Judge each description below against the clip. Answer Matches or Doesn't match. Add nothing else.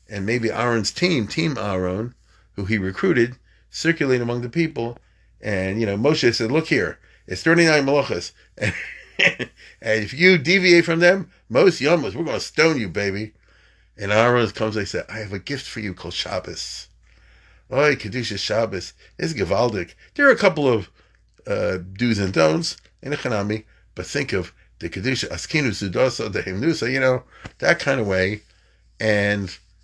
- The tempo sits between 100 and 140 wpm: Doesn't match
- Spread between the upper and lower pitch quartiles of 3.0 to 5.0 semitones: Doesn't match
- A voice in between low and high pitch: Doesn't match